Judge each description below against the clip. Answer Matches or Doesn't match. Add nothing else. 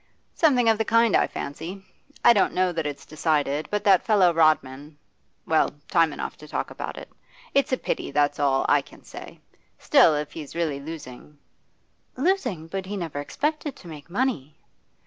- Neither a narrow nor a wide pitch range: Doesn't match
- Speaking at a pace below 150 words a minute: Doesn't match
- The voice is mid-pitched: Matches